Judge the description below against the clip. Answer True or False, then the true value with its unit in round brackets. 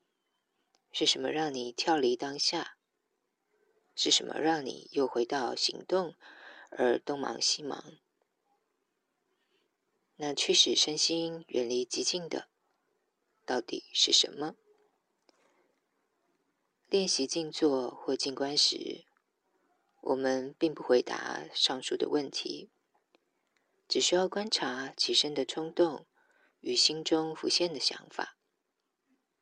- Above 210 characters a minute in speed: False (155 characters per minute)